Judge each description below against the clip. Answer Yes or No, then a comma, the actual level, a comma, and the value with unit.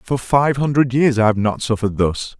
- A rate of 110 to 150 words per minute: No, fast, 225 wpm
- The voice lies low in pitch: Yes, low, 120 Hz